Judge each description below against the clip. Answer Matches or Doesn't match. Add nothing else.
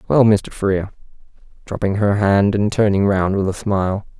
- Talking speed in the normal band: Matches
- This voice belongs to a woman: Doesn't match